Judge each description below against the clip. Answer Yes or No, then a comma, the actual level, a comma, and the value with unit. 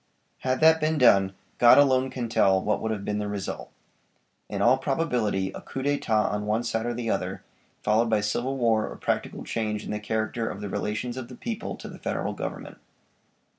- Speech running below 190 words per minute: No, fast, 205 wpm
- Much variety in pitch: No, average, 3.5 semitones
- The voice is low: Yes, low, 115 Hz